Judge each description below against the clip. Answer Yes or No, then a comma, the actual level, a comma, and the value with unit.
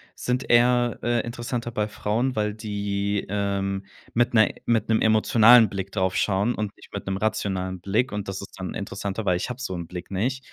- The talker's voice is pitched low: Yes, low, 105 Hz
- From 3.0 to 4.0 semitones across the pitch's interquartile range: Yes, average, 3.3 semitones